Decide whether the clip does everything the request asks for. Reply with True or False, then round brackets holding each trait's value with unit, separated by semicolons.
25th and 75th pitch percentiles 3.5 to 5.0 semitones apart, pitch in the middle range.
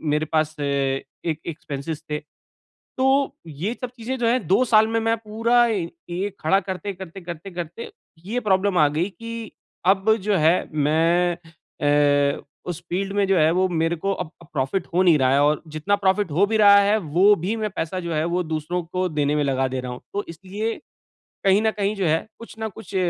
True (4.7 semitones; 180 Hz)